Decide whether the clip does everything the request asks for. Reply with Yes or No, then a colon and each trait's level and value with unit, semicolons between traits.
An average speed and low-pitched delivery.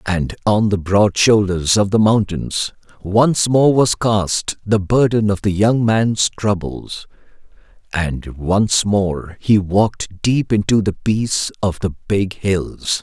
Yes: average, 145 wpm; low, 100 Hz